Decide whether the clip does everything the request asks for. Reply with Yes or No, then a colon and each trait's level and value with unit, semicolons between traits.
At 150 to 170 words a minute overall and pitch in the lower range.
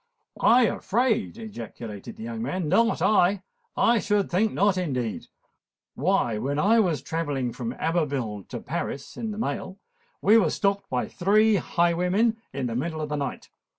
No: average, 160 wpm; medium, 180 Hz